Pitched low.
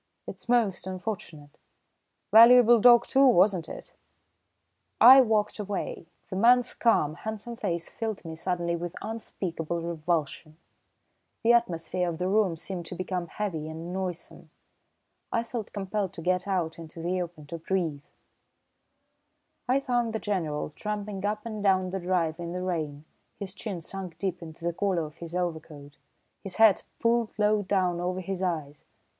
No: medium, 185 Hz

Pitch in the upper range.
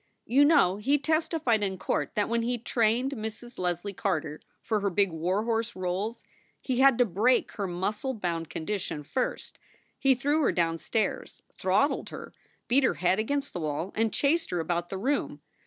Yes: high, 215 Hz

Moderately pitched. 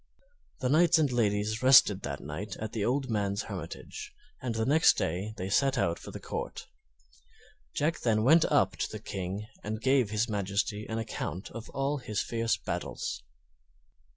No: low, 110 Hz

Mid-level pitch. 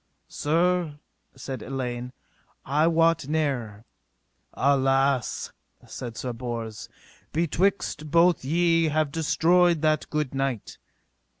Yes: medium, 145 Hz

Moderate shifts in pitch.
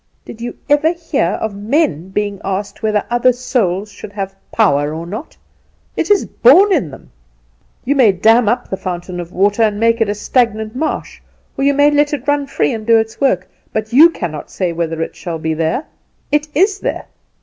No: wide, 6.7 semitones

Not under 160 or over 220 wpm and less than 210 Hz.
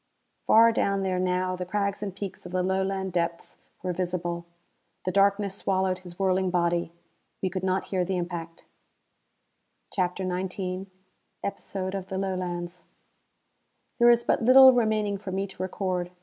No: average, 150 wpm; medium, 185 Hz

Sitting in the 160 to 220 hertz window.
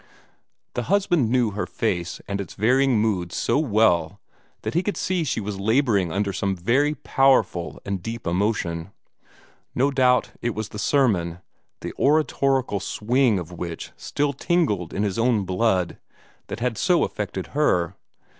No: low, 110 Hz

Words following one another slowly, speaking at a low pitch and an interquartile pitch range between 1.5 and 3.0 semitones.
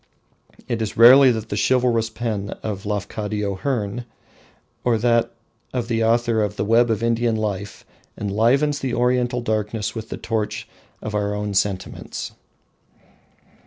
No: average, 145 wpm; low, 110 Hz; narrow, 2.4 semitones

